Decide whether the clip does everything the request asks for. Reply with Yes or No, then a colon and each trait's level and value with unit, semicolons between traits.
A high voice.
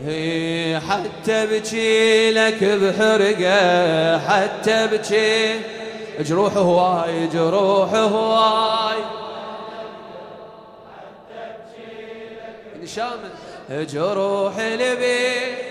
Yes: high, 220 Hz